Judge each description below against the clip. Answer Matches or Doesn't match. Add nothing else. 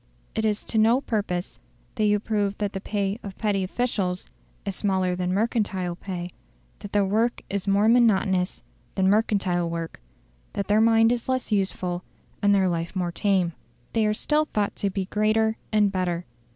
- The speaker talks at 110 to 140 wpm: Doesn't match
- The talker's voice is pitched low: Doesn't match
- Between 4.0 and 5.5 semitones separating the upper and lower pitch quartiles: Doesn't match